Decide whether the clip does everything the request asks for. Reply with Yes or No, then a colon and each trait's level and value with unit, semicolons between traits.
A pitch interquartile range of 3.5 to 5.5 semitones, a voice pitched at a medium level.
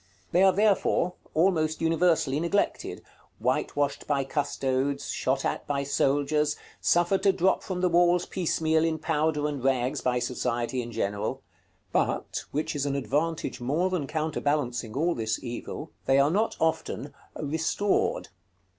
Yes: average, 3.8 semitones; medium, 150 Hz